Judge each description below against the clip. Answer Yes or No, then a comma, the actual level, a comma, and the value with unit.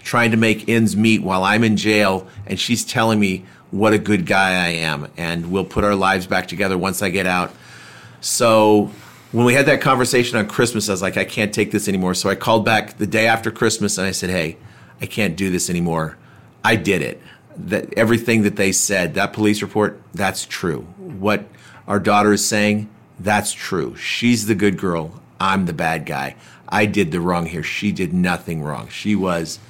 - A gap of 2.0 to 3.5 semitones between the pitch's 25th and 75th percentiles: Yes, average, 2.8 semitones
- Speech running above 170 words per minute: Yes, fast, 205 wpm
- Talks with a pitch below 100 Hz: No, low, 105 Hz